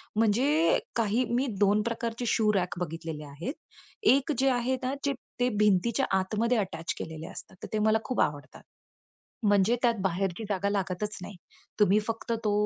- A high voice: Yes, high, 210 Hz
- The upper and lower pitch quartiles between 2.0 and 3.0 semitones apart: No, average, 4.1 semitones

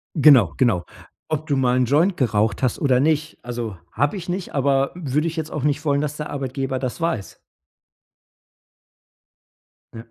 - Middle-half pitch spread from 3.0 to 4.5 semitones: Yes, average, 3.4 semitones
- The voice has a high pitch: No, medium, 140 Hz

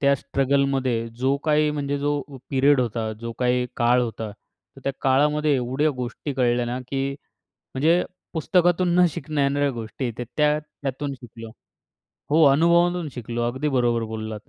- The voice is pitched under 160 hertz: Yes, low, 135 Hz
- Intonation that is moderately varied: Yes, average, 3.4 semitones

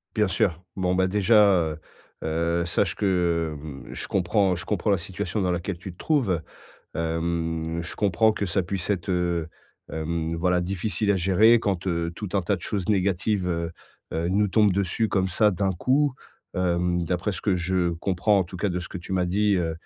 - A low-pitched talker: Yes, very low, 90 Hz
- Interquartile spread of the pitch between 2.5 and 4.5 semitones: Yes, average, 2.8 semitones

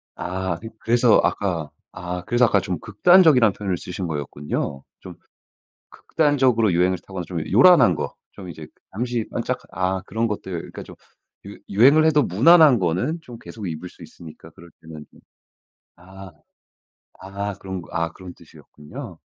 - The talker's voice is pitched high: No, very low, 95 Hz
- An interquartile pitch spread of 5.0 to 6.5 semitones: Yes, wide, 5.4 semitones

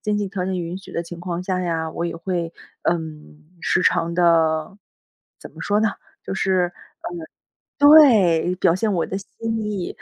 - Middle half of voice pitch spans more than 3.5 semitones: No, average, 2.9 semitones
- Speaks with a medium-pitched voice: Yes, medium, 180 Hz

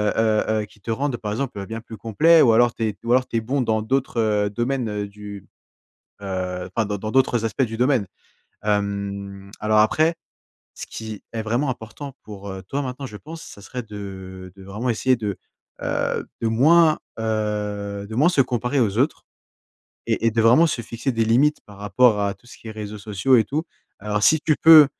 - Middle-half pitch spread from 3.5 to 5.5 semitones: Yes, average, 3.8 semitones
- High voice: No, low, 110 Hz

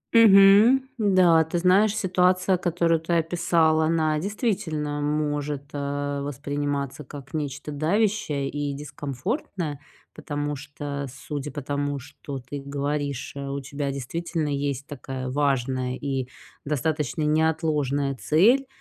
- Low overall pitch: No, medium, 145 Hz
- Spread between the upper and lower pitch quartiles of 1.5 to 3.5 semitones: Yes, average, 2.9 semitones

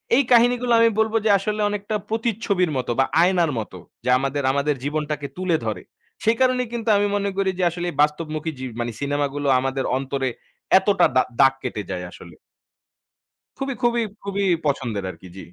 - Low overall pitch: No, medium, 160 Hz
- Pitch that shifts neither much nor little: No, wide, 7.8 semitones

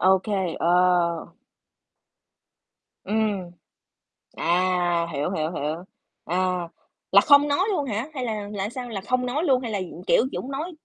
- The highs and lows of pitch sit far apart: Yes, wide, 6.1 semitones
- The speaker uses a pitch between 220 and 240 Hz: No, high, 205 Hz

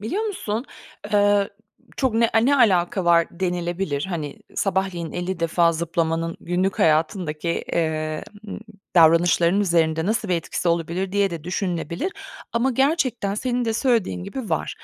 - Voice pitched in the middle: Yes, medium, 180 Hz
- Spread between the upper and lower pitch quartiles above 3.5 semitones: Yes, average, 4.5 semitones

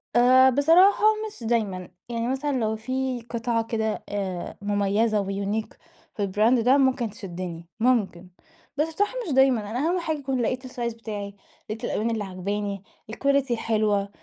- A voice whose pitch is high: Yes, high, 230 Hz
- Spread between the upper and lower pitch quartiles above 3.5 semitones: Yes, average, 4.2 semitones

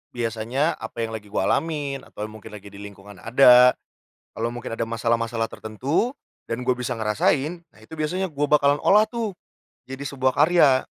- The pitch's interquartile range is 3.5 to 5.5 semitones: Yes, average, 4.7 semitones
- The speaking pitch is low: Yes, low, 125 Hz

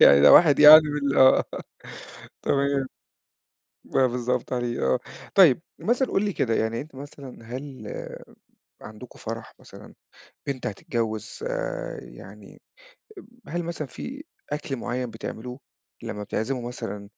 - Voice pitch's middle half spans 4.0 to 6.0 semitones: Yes, average, 4.4 semitones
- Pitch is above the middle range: No, low, 130 Hz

